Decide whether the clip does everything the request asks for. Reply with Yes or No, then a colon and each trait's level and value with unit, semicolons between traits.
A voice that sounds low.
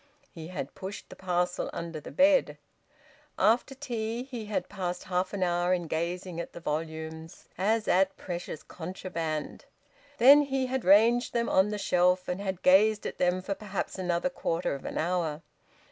No: medium, 185 Hz